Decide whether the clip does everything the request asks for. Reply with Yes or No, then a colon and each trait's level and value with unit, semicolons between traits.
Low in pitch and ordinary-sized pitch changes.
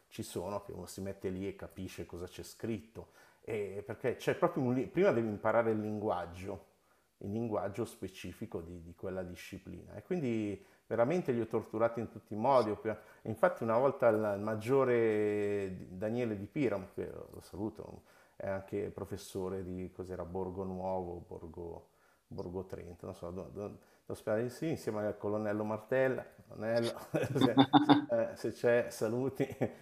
Yes: low, 105 Hz; average, 3.6 semitones